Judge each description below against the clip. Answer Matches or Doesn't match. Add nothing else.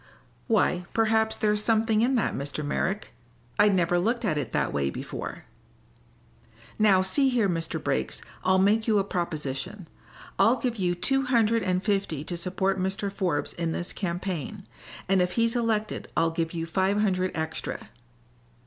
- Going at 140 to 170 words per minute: Matches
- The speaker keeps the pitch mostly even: Doesn't match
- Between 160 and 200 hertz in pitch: Matches